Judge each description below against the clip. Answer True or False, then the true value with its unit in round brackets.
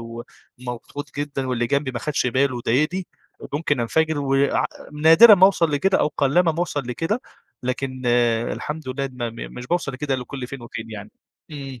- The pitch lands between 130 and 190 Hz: True (135 Hz)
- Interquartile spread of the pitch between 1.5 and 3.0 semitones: False (3.7 semitones)